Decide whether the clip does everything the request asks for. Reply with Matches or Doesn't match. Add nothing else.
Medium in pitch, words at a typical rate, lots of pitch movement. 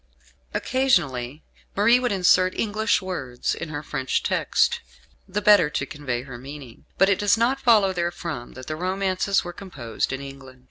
Matches